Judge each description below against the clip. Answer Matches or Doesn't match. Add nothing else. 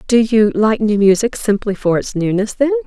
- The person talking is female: Matches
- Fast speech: Matches